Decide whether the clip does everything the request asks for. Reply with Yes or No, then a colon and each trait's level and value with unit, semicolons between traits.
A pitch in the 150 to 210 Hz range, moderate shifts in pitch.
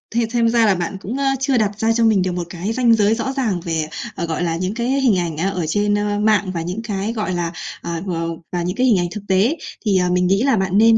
Yes: high, 205 Hz; average, 4.0 semitones